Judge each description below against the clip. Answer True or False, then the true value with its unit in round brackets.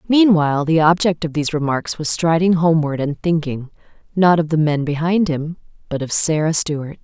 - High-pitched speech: False (160 Hz)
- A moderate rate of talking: True (180 wpm)